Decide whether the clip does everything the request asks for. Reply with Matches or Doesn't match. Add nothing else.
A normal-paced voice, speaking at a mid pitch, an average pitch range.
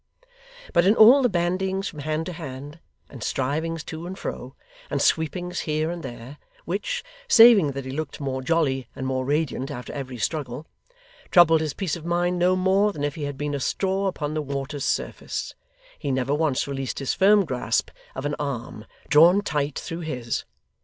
Matches